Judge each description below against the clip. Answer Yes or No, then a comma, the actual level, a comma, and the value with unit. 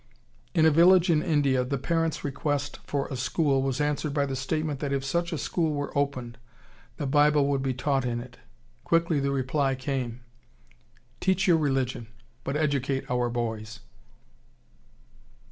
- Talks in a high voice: No, medium, 140 Hz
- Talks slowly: No, average, 160 wpm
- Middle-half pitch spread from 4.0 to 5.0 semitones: No, narrow, 2.6 semitones